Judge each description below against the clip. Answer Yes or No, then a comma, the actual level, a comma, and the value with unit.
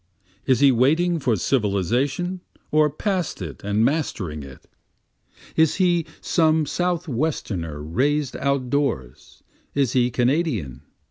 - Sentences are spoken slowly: Yes, slow, 115 wpm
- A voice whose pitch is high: No, low, 135 Hz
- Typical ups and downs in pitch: No, wide, 7.5 semitones